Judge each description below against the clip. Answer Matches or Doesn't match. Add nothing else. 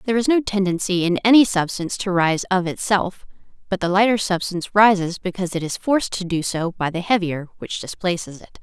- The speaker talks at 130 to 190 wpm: Doesn't match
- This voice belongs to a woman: Matches